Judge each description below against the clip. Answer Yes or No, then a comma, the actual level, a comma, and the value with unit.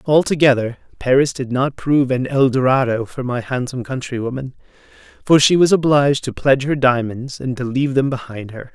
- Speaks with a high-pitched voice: No, low, 130 Hz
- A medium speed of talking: Yes, average, 180 wpm